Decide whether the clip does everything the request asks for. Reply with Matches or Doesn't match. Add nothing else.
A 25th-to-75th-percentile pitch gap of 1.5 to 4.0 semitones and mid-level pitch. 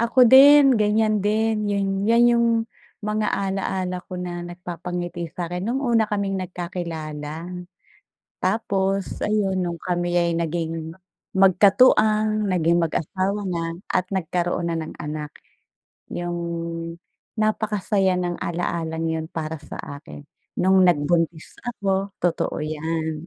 Matches